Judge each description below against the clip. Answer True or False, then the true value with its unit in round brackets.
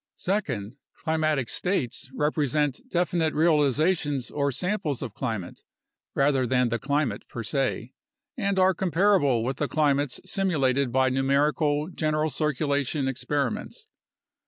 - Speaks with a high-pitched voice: False (145 Hz)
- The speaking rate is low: True (120 wpm)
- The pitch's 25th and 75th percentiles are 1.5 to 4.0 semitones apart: True (3.2 semitones)